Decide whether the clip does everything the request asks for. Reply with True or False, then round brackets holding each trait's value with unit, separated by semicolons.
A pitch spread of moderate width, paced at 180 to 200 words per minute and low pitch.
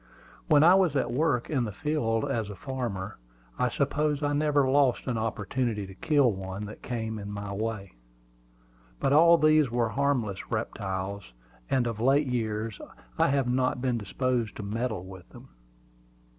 False (5.0 semitones; 165 wpm; 120 Hz)